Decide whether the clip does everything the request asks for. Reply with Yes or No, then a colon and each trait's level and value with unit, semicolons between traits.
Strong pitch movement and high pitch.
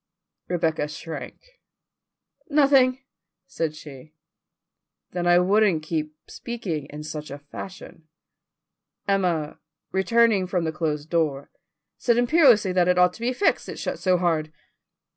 No: wide, 5.8 semitones; medium, 175 Hz